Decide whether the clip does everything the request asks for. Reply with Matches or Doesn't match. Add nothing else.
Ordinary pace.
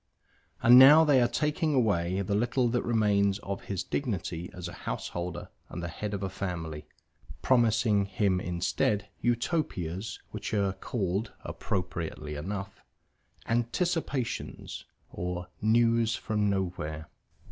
Doesn't match